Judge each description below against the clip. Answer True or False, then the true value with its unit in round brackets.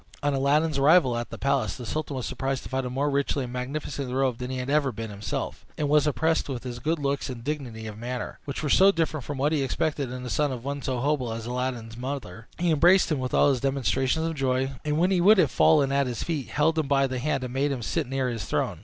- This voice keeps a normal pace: False (265 wpm)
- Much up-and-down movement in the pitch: False (3.0 semitones)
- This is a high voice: False (135 Hz)